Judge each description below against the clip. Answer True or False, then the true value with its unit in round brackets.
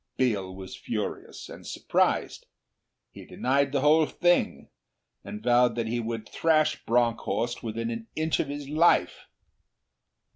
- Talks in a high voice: False (120 Hz)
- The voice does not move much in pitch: False (4.7 semitones)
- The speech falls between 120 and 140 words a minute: True (135 wpm)